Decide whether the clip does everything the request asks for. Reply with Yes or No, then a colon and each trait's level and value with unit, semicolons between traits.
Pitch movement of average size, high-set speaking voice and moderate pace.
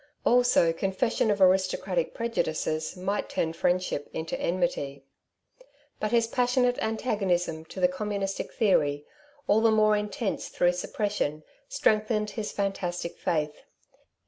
No: average, 4.1 semitones; high, 195 Hz; slow, 120 wpm